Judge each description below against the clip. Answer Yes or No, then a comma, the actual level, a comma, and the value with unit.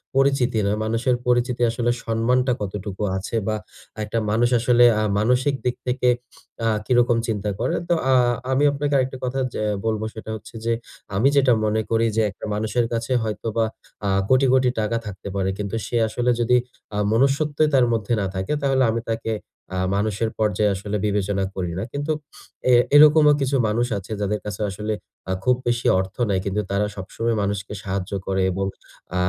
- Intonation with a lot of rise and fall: No, average, 3.4 semitones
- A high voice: No, low, 115 Hz